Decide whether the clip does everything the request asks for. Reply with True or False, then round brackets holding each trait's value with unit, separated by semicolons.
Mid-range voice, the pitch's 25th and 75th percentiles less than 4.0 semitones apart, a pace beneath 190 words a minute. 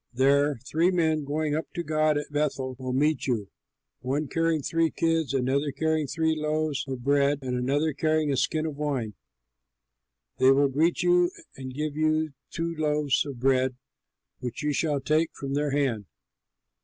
True (145 Hz; 2.7 semitones; 165 wpm)